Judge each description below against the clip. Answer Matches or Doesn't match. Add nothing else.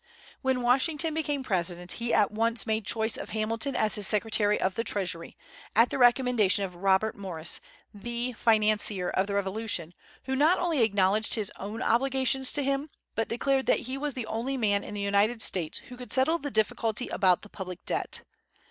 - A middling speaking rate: Matches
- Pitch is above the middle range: Matches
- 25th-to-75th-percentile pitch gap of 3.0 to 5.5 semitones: Matches